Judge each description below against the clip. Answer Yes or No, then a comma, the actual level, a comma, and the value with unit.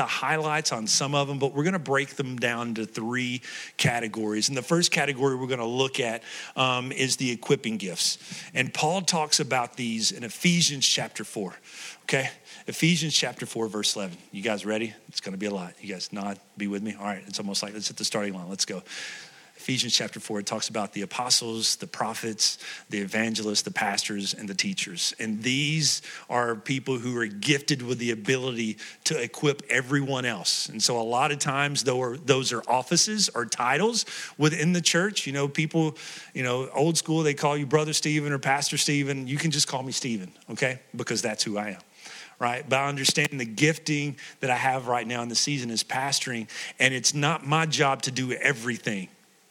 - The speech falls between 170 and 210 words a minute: Yes, fast, 205 wpm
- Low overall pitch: Yes, low, 130 Hz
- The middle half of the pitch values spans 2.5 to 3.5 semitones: No, average, 4.5 semitones